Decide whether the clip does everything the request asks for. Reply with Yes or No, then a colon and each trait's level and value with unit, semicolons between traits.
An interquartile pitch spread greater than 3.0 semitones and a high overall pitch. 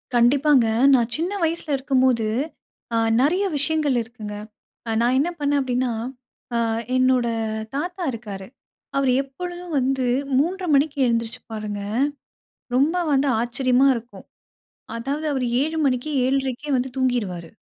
Yes: average, 3.4 semitones; very high, 265 Hz